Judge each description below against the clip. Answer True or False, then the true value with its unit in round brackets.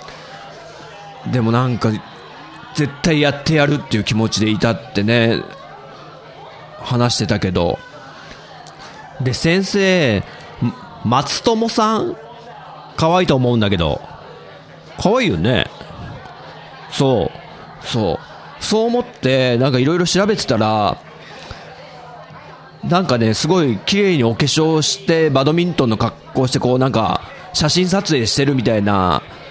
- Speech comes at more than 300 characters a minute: False (230 characters per minute)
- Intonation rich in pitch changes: True (7.0 semitones)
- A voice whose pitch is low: True (130 Hz)